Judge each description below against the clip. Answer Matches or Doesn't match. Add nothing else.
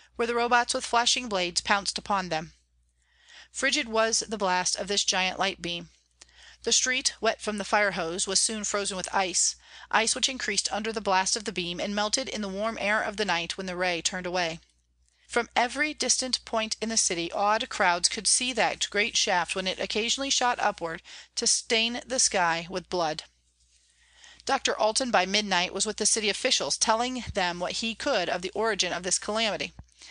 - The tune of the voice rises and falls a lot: Doesn't match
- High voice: Matches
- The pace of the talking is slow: Doesn't match